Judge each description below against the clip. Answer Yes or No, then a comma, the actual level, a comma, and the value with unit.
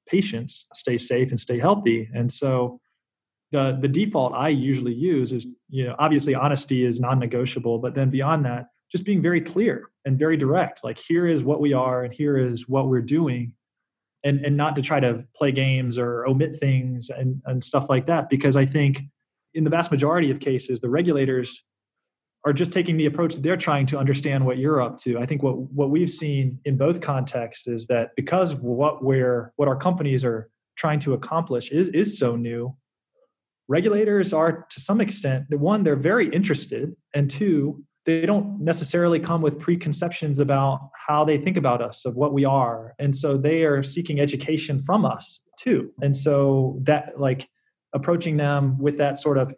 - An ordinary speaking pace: Yes, average, 190 wpm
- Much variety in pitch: No, average, 3.6 semitones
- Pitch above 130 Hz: Yes, medium, 140 Hz